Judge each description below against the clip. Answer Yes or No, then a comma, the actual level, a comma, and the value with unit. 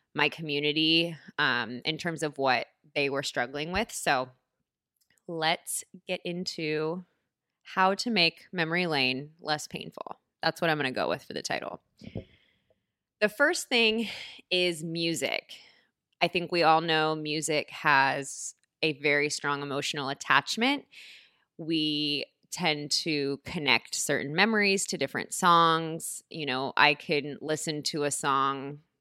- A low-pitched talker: No, medium, 155 Hz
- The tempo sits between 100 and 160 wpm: Yes, slow, 135 wpm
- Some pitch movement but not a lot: Yes, average, 3.3 semitones